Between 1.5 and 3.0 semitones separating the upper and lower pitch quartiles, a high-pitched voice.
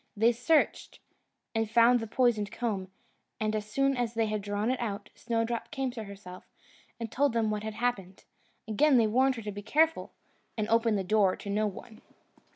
Yes: narrow, 2.6 semitones; high, 225 Hz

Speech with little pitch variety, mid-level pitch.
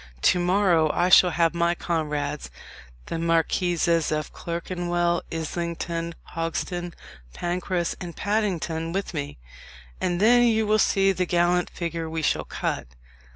Yes: narrow, 1.7 semitones; medium, 175 Hz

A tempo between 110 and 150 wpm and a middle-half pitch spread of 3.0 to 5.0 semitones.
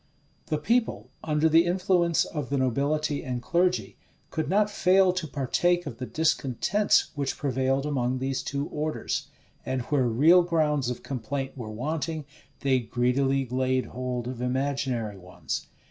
Yes: average, 145 wpm; average, 4.0 semitones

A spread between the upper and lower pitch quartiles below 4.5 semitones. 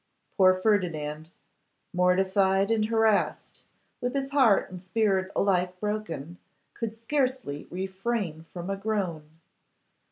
Yes: average, 3.5 semitones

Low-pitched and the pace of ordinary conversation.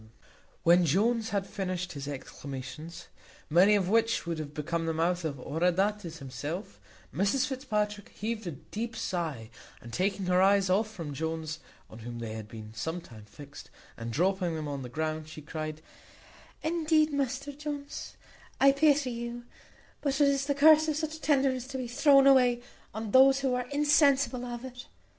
No: high, 195 Hz; average, 170 wpm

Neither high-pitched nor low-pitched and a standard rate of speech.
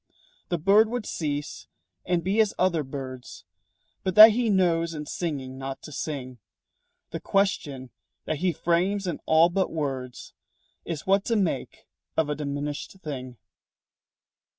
Yes: medium, 160 Hz; average, 145 wpm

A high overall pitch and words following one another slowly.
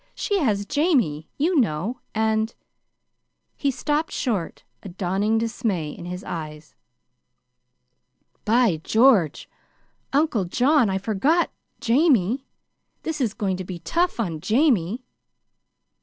Yes: high, 220 Hz; slow, 115 wpm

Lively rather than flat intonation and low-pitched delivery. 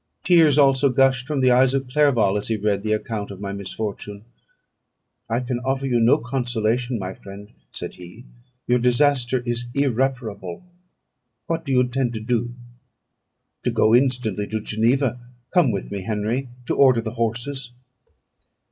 No: average, 3.5 semitones; low, 120 Hz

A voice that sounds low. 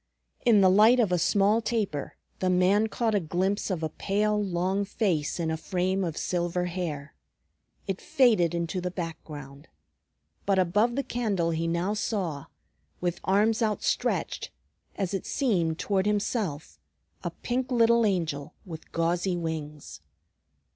No: medium, 185 Hz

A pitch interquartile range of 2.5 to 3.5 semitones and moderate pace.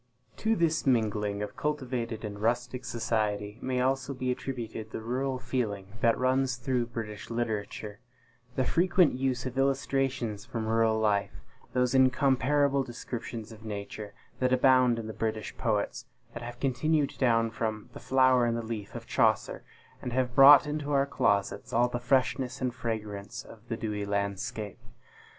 Yes: average, 3.1 semitones; average, 155 wpm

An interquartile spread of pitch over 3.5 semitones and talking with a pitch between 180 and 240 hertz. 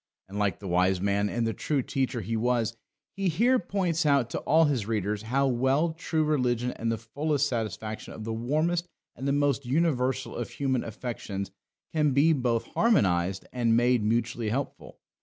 No: average, 4.7 semitones; low, 125 Hz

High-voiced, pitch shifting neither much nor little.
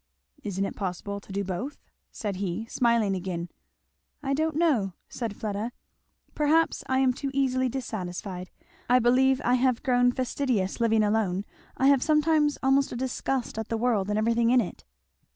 Yes: high, 235 Hz; average, 4.7 semitones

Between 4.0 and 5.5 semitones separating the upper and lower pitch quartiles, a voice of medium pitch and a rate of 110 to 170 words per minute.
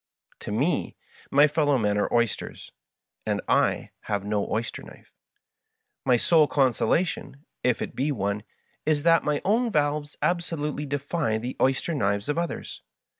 Yes: average, 5.1 semitones; medium, 145 Hz; average, 150 wpm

